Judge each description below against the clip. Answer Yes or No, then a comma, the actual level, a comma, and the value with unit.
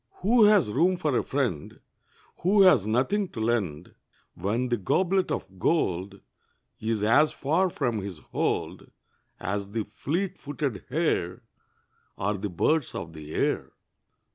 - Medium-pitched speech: No, low, 115 Hz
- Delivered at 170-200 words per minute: No, average, 140 wpm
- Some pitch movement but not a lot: No, wide, 8.9 semitones